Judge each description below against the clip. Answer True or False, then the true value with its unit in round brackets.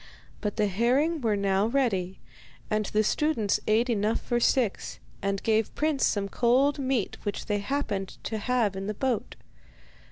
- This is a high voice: True (220 Hz)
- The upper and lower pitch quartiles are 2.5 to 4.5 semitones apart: True (4.1 semitones)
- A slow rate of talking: False (160 wpm)